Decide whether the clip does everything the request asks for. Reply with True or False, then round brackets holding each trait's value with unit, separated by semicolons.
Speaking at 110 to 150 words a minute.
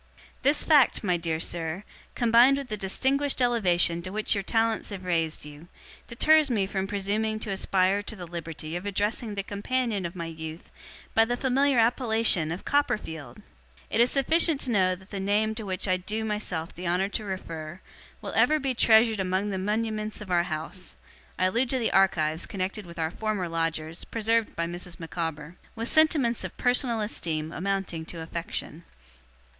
False (180 wpm)